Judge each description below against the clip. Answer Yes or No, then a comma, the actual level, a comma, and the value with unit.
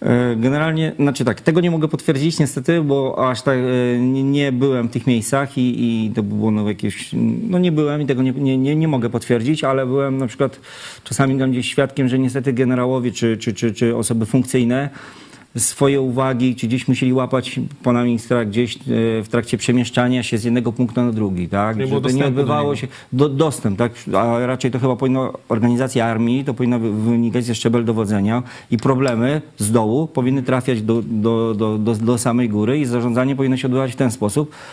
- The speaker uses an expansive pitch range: No, narrow, 2.5 semitones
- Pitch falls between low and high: No, low, 125 Hz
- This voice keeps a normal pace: No, fast, 190 wpm